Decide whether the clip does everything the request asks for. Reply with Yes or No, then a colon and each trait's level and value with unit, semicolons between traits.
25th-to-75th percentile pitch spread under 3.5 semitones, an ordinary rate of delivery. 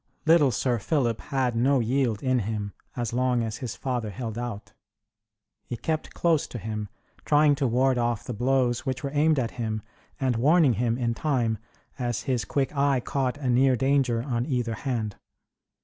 Yes: average, 2.8 semitones; average, 180 wpm